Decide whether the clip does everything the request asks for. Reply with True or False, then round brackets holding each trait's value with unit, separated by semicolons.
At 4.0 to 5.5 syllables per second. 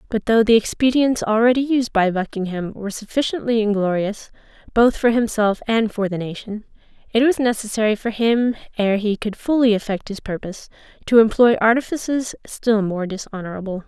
True (5.4 syllables/s)